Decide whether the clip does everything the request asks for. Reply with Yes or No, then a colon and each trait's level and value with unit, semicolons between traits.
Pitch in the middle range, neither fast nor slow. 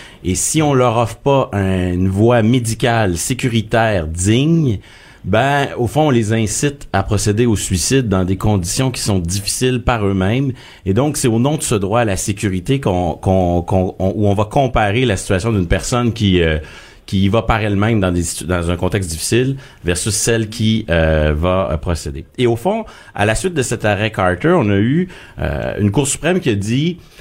No: low, 110 Hz; average, 200 wpm